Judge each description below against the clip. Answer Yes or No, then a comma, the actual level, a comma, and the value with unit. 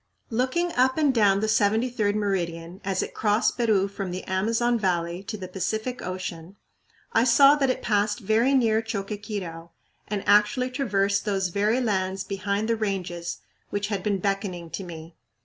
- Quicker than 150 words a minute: Yes, average, 165 wpm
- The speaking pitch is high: Yes, high, 205 Hz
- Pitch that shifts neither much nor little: Yes, average, 3.1 semitones